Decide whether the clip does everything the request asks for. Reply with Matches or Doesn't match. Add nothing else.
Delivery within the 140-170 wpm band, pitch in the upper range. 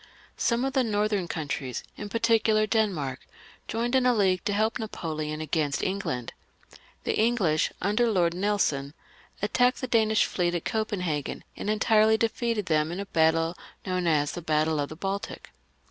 Matches